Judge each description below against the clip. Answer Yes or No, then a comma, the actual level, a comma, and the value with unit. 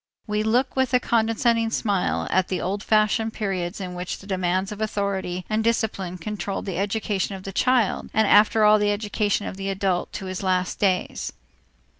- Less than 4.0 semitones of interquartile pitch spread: Yes, average, 2.7 semitones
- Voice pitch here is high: Yes, high, 205 Hz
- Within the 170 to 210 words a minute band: Yes, average, 185 wpm